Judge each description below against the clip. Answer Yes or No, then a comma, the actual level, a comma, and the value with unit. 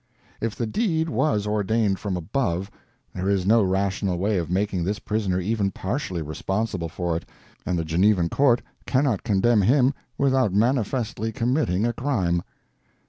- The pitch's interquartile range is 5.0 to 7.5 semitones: No, average, 4.3 semitones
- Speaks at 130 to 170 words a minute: Yes, average, 150 wpm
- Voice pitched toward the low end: Yes, low, 105 Hz